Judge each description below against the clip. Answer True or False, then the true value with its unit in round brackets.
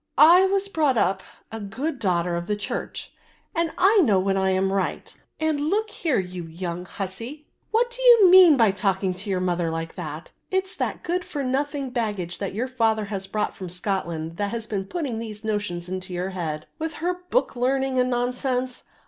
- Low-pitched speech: False (220 Hz)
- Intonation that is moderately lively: False (7.8 semitones)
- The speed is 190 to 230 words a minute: True (195 wpm)